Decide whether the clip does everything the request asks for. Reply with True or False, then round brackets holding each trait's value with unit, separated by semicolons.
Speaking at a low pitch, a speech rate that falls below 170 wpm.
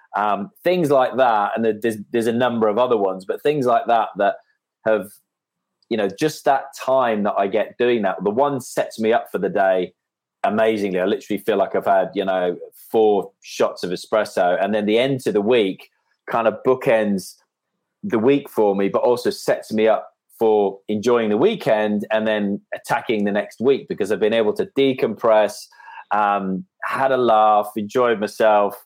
False (110 Hz; 185 wpm)